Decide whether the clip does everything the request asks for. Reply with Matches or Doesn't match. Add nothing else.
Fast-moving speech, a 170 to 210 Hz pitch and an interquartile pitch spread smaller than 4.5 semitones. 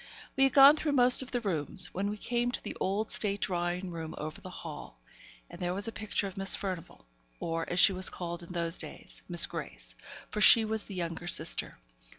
Matches